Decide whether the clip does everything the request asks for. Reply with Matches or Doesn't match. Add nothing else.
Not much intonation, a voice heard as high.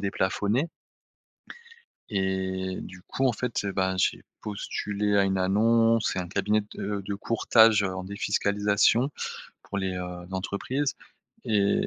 Doesn't match